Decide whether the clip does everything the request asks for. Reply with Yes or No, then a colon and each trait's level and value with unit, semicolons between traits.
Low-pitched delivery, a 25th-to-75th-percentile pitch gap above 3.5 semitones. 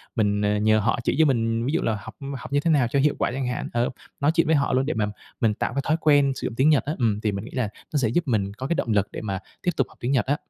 Yes: low, 125 Hz; average, 4.7 semitones